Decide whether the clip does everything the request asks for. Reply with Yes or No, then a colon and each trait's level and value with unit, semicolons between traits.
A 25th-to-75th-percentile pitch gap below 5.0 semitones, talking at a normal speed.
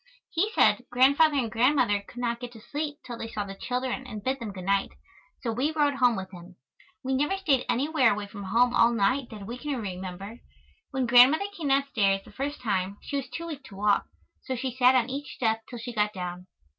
No: average, 4.6 semitones; fast, 220 wpm